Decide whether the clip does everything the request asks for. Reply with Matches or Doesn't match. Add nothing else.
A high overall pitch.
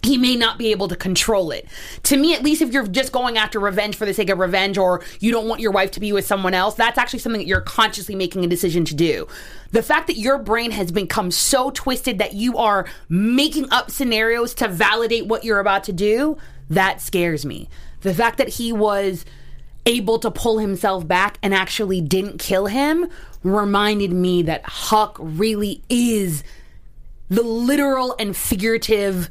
Matches